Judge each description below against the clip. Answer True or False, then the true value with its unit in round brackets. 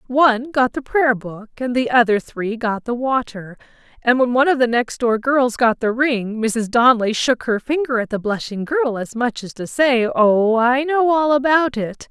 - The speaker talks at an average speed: False (215 wpm)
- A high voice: True (245 Hz)